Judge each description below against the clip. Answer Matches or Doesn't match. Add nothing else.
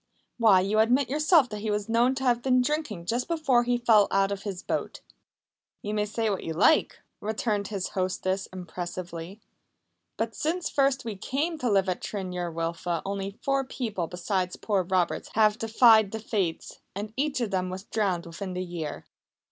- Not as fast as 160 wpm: Doesn't match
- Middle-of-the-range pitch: Doesn't match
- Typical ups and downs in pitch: Matches